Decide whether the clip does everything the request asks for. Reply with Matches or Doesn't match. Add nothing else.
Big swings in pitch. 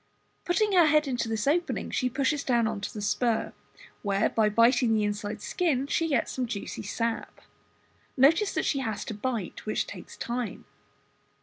Doesn't match